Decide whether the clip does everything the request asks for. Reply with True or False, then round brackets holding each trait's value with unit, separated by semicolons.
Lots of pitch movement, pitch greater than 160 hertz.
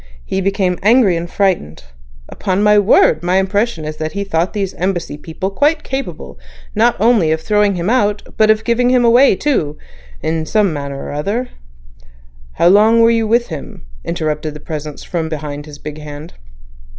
True (5.7 semitones; 190 Hz)